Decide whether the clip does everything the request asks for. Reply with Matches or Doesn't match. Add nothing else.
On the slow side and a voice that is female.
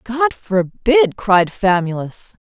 Matches